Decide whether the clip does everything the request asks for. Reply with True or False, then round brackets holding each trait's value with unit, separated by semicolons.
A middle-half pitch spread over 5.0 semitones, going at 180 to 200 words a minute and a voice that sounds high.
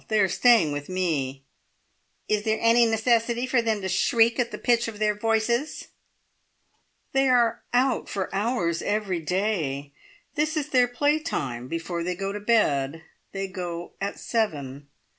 False (5.6 semitones; 160 wpm; 210 Hz)